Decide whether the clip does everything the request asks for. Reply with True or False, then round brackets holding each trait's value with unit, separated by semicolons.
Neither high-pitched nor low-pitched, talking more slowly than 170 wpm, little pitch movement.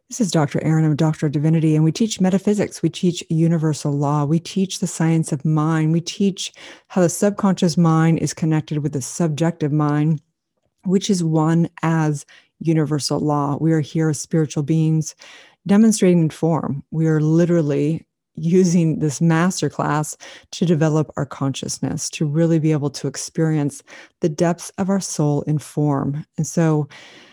True (160 Hz; 160 wpm; 2.1 semitones)